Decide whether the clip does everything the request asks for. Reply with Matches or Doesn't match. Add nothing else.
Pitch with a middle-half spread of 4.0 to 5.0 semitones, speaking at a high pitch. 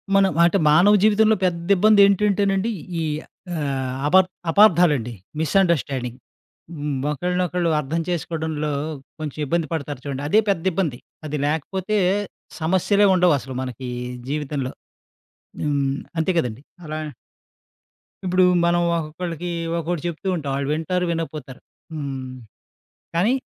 Doesn't match